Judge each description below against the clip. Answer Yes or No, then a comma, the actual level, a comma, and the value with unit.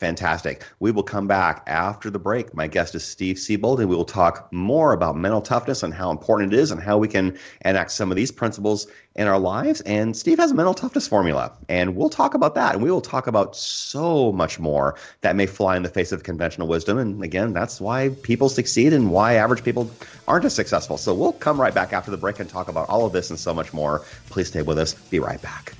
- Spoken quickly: Yes, fast, 245 wpm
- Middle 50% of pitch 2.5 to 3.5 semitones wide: No, average, 4.5 semitones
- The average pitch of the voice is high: No, low, 100 Hz